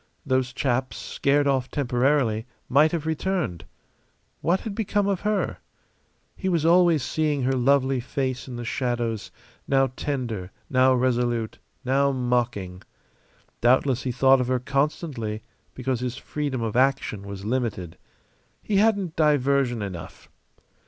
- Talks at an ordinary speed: No, slow, 130 wpm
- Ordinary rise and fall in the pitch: Yes, average, 3.3 semitones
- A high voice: No, low, 130 Hz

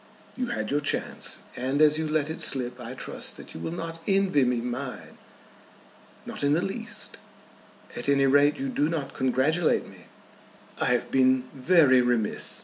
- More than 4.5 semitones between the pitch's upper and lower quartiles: No, average, 4.2 semitones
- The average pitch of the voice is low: No, medium, 145 Hz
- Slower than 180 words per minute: Yes, average, 170 wpm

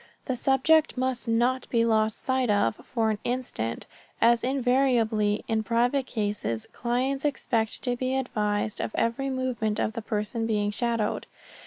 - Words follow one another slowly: No, average, 150 wpm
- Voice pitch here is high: Yes, high, 235 Hz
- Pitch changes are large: No, average, 3.0 semitones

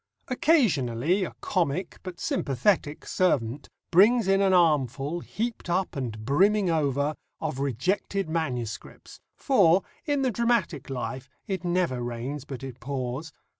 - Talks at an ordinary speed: No, slow, 130 wpm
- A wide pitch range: Yes, wide, 6.5 semitones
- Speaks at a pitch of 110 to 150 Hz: No, medium, 160 Hz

